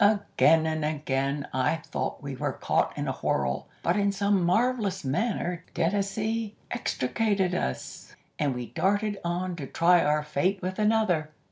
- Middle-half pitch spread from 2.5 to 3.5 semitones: No, average, 5.2 semitones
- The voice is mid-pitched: Yes, medium, 180 Hz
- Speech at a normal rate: Yes, average, 150 wpm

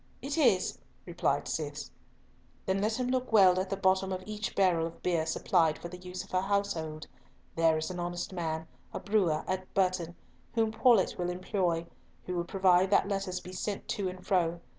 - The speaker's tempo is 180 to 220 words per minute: Yes, average, 190 wpm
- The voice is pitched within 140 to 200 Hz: Yes, medium, 185 Hz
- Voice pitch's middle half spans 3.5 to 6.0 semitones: No, narrow, 2.4 semitones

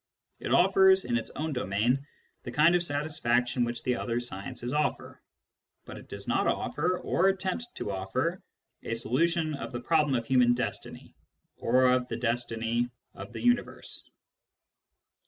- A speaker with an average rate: Yes, average, 155 wpm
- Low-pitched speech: Yes, low, 130 Hz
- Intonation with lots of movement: Yes, wide, 5.7 semitones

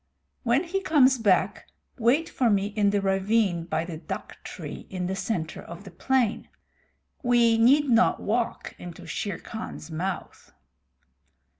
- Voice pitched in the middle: No, high, 210 Hz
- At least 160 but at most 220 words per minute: No, average, 145 wpm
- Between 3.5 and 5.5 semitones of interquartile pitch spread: Yes, average, 4.7 semitones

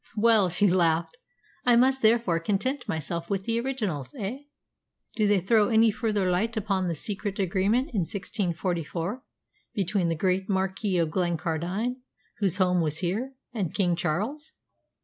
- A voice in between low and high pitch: No, high, 195 Hz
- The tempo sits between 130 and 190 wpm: Yes, average, 150 wpm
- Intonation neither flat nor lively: Yes, average, 4.2 semitones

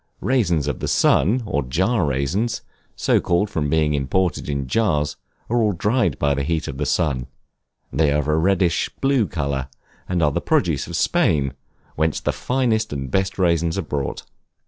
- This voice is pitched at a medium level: No, very low, 80 Hz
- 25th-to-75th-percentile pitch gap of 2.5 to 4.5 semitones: No, wide, 5.4 semitones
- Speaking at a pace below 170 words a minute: No, average, 180 wpm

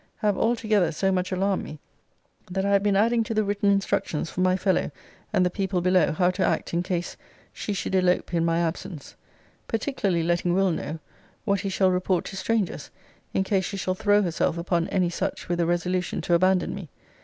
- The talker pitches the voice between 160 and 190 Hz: Yes, medium, 185 Hz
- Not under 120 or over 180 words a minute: No, fast, 205 wpm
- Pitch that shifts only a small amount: Yes, narrow, 2.3 semitones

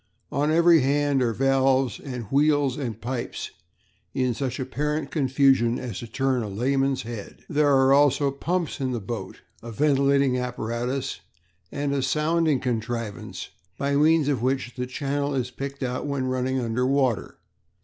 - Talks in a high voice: No, low, 135 Hz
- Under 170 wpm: Yes, average, 155 wpm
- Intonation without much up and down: Yes, narrow, 2.3 semitones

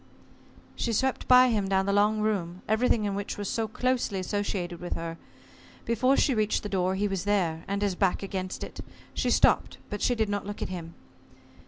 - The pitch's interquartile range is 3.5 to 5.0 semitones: No, narrow, 2.6 semitones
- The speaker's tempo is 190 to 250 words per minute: Yes, average, 200 wpm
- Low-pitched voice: No, high, 205 Hz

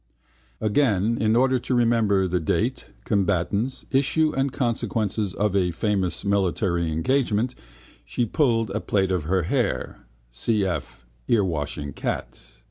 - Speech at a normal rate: No, slow, 125 wpm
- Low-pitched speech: Yes, low, 105 Hz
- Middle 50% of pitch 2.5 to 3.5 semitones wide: No, average, 4.4 semitones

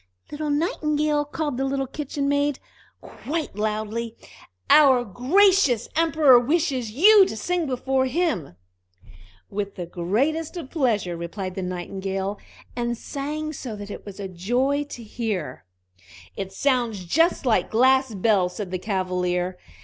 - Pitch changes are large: Yes, wide, 6.9 semitones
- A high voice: Yes, high, 245 Hz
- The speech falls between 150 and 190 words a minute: No, slow, 135 wpm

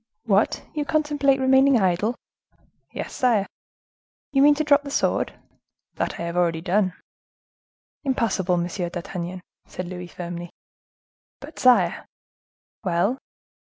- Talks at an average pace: No, slow, 120 wpm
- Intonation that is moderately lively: No, wide, 7.3 semitones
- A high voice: Yes, high, 200 Hz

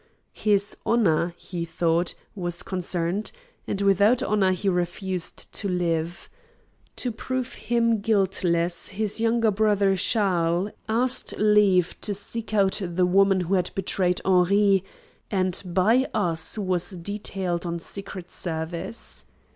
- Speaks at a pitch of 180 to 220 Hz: Yes, high, 190 Hz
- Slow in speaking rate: Yes, slow, 125 wpm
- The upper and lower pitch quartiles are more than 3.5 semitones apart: No, average, 3.0 semitones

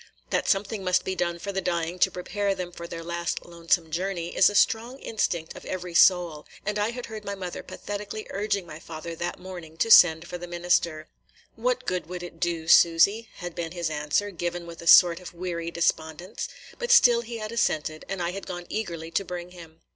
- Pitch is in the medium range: Yes, medium, 175 Hz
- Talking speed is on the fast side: Yes, fast, 210 wpm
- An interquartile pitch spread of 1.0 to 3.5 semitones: Yes, average, 2.7 semitones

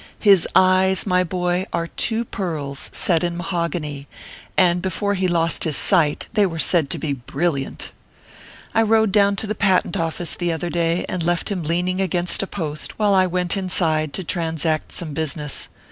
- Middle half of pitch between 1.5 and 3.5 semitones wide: Yes, average, 2.7 semitones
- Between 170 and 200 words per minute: Yes, average, 175 wpm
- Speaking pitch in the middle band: Yes, medium, 175 Hz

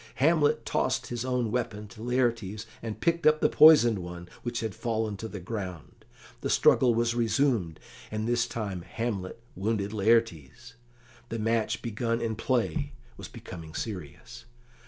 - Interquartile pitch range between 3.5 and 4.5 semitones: No, average, 2.8 semitones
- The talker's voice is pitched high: No, low, 115 Hz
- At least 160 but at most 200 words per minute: No, average, 150 wpm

